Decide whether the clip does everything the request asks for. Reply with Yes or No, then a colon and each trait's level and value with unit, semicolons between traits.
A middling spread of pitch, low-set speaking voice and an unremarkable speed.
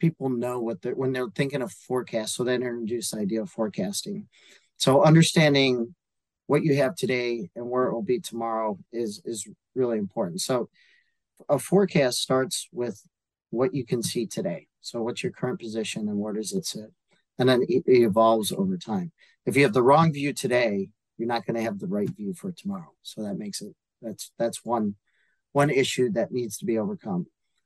No: wide, 8.5 semitones; low, 130 Hz; average, 195 wpm